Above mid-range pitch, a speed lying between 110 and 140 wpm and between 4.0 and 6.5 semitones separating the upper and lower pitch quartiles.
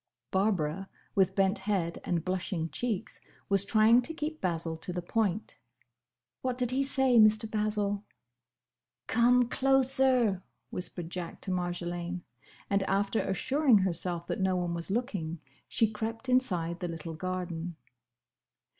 Yes: high, 195 Hz; slow, 135 wpm; average, 4.6 semitones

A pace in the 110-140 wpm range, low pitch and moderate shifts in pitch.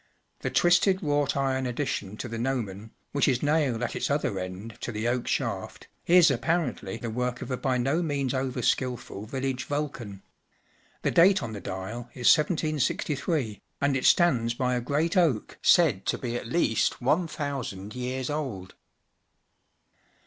No: average, 165 wpm; low, 130 Hz; average, 4.1 semitones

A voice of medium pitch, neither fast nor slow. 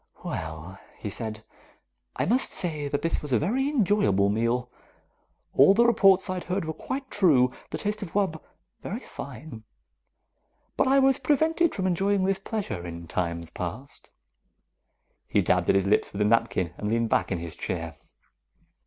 Yes: medium, 150 Hz; average, 170 wpm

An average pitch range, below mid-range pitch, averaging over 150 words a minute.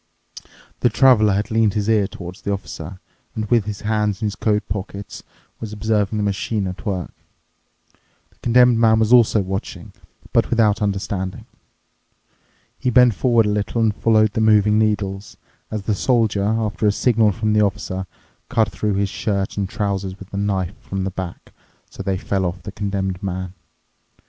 No: narrow, 2.1 semitones; low, 105 Hz; average, 175 wpm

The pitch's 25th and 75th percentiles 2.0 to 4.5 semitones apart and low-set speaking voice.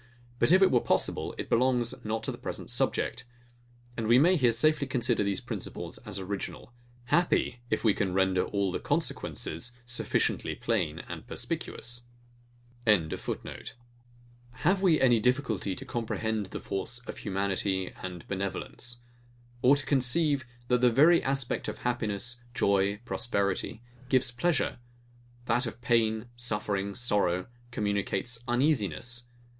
Yes: average, 3.8 semitones; low, 120 Hz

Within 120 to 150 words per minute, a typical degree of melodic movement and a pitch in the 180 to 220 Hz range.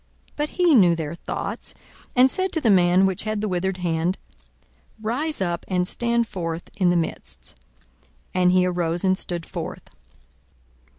No: average, 165 wpm; average, 4.1 semitones; medium, 185 Hz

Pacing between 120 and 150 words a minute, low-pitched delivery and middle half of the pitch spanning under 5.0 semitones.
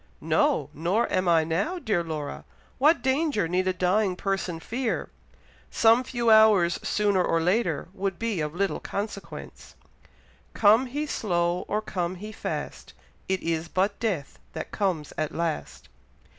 No: average, 145 wpm; high, 195 Hz; average, 4.3 semitones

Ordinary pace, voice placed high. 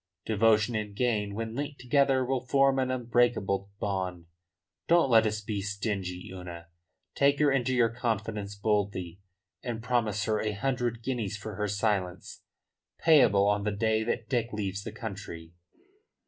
No: average, 150 wpm; low, 110 Hz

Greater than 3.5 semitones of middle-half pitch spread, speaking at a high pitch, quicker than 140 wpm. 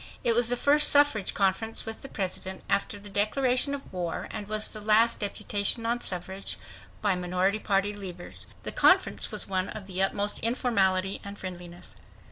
No: average, 3.2 semitones; high, 205 Hz; average, 170 wpm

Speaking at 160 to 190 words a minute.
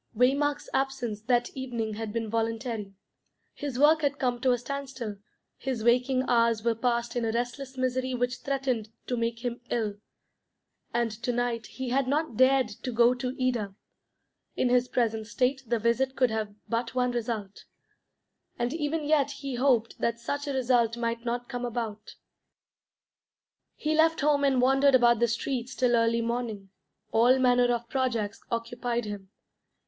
Yes: average, 165 wpm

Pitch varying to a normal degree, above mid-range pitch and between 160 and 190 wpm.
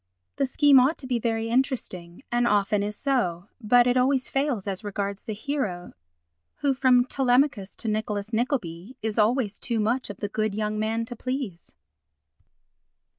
Yes: average, 3.8 semitones; high, 230 Hz; average, 165 wpm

